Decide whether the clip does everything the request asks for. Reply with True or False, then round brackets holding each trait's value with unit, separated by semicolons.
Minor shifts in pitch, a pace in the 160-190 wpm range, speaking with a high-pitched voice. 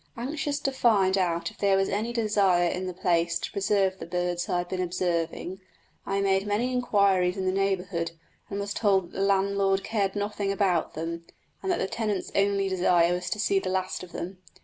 False (2.1 semitones; 205 wpm; 195 Hz)